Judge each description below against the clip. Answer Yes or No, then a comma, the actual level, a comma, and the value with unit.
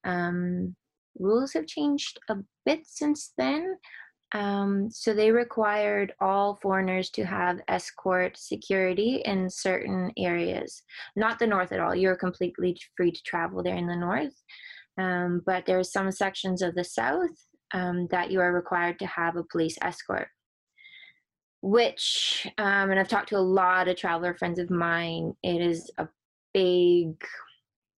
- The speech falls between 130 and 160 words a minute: Yes, average, 155 wpm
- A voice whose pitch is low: No, high, 190 Hz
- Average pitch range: Yes, average, 3.4 semitones